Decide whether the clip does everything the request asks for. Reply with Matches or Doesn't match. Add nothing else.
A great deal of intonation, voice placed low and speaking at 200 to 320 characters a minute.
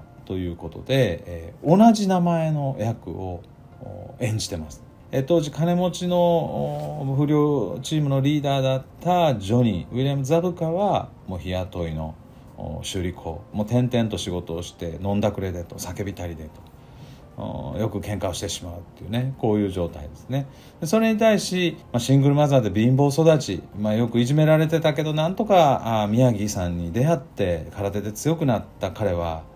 Doesn't match